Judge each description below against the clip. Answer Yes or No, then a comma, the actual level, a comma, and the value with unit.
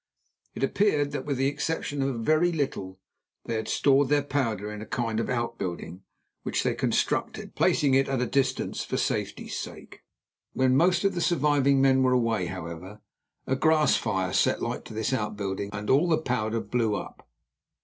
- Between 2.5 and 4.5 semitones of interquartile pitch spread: No, average, 5.1 semitones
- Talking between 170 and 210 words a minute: Yes, average, 180 wpm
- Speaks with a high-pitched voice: No, low, 130 Hz